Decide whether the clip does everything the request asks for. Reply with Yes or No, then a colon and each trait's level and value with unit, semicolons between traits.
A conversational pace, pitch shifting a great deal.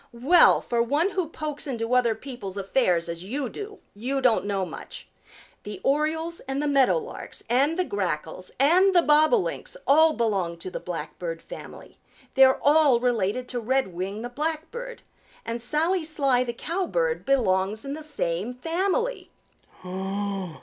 Yes: average, 150 wpm; wide, 6.8 semitones